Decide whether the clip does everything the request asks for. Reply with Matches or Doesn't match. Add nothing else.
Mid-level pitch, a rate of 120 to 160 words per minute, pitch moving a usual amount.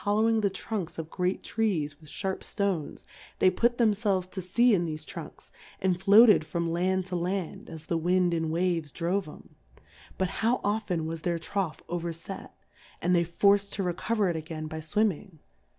Doesn't match